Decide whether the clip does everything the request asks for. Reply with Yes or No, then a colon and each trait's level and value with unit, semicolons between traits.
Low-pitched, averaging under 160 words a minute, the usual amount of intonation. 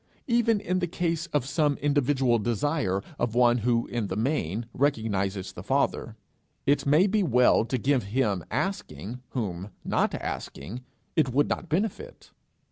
No: low, 130 Hz; average, 150 wpm; wide, 5.8 semitones